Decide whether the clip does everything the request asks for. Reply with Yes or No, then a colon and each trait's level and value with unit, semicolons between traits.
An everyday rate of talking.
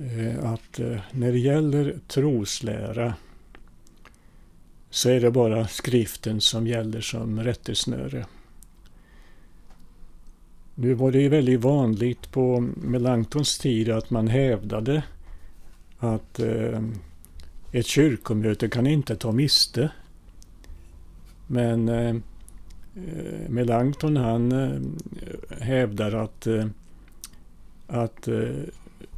No: slow, 75 wpm